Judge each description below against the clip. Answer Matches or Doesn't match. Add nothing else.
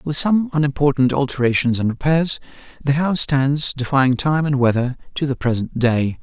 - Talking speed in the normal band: Matches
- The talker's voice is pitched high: Doesn't match